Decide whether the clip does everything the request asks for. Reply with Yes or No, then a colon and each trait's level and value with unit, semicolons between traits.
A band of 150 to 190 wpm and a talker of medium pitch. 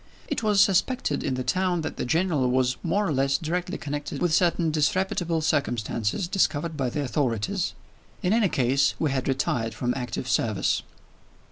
Yes: average, 165 wpm; medium, 150 Hz